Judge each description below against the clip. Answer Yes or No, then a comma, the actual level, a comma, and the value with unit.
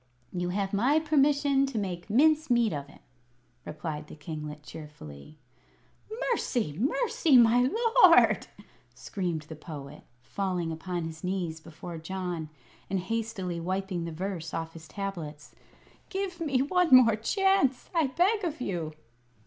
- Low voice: No, high, 190 Hz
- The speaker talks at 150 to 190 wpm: No, slow, 135 wpm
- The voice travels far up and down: Yes, wide, 8.7 semitones